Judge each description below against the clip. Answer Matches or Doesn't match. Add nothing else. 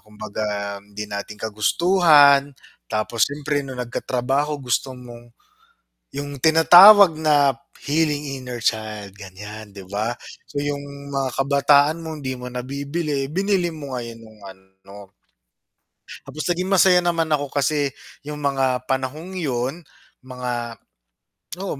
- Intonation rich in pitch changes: Doesn't match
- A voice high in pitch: Doesn't match